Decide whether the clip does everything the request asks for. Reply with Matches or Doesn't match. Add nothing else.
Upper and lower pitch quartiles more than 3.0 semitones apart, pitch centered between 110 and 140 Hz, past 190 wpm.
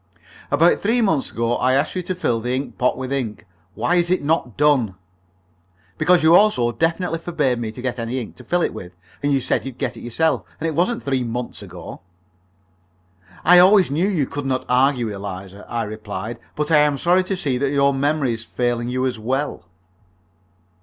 Matches